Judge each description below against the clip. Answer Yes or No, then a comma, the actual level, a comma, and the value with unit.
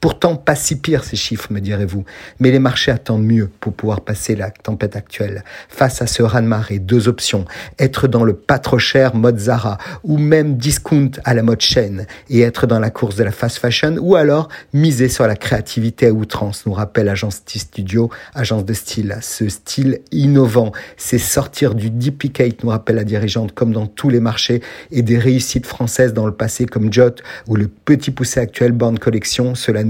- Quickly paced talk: No, average, 190 wpm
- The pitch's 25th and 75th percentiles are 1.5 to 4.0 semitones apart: Yes, average, 3.1 semitones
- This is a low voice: Yes, low, 120 Hz